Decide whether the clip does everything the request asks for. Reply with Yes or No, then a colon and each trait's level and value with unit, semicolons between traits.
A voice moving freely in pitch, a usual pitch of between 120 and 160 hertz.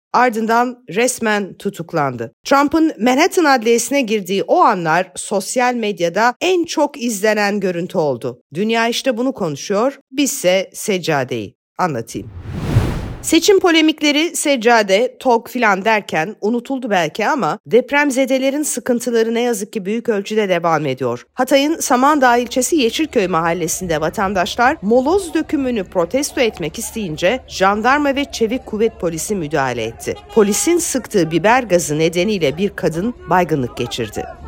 No: wide, 6.6 semitones; high, 225 Hz